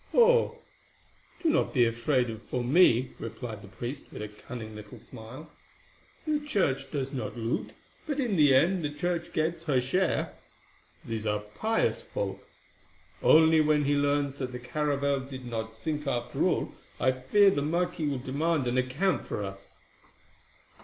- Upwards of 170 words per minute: No, average, 160 wpm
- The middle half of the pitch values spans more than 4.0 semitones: Yes, average, 5.0 semitones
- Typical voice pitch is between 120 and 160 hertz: Yes, medium, 140 Hz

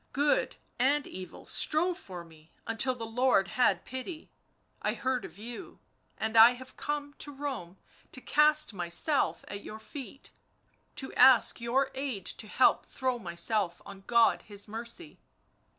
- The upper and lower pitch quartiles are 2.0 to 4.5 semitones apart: No, average, 5.1 semitones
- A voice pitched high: Yes, high, 245 Hz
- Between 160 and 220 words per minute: No, average, 150 wpm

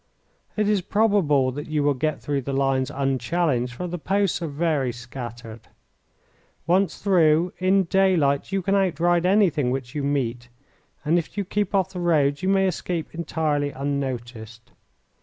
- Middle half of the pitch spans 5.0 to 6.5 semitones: Yes, average, 5.3 semitones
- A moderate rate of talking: Yes, average, 160 wpm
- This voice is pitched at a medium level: Yes, medium, 150 Hz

